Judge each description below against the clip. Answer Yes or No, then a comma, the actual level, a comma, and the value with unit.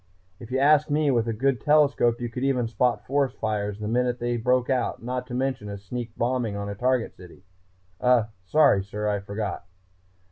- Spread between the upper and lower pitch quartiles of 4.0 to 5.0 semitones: No, average, 3.4 semitones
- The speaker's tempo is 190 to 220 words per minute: Yes, average, 200 wpm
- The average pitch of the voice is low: Yes, low, 120 Hz